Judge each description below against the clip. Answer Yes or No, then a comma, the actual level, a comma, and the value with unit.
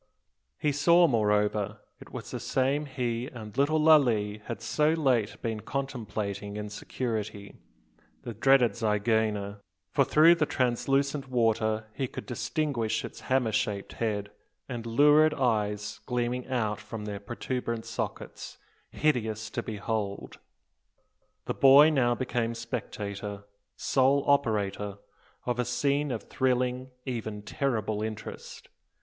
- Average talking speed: No, slow, 125 wpm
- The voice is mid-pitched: No, low, 115 Hz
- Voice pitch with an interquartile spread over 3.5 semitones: Yes, average, 4.1 semitones